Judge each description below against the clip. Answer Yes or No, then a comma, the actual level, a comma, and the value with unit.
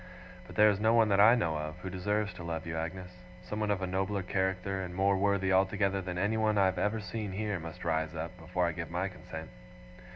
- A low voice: Yes, very low, 95 Hz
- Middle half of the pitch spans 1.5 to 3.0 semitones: Yes, narrow, 2.5 semitones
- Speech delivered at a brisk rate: Yes, fast, 230 wpm